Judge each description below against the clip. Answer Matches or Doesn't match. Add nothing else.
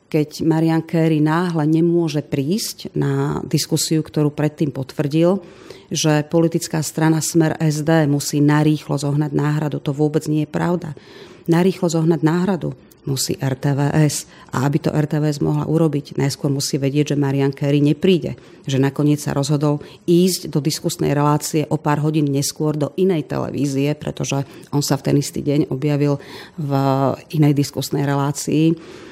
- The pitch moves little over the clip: Matches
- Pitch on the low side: Doesn't match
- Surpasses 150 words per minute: Doesn't match